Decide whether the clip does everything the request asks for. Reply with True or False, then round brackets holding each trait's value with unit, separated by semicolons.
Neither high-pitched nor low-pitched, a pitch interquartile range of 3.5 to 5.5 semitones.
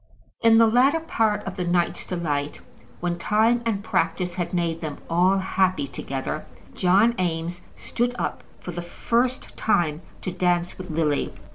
True (180 Hz; 4.2 semitones)